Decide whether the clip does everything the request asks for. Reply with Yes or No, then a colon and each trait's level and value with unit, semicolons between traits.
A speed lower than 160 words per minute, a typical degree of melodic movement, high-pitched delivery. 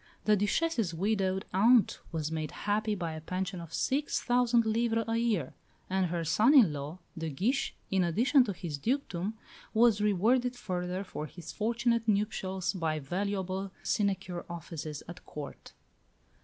Yes: average, 150 wpm; average, 4.8 semitones; high, 195 Hz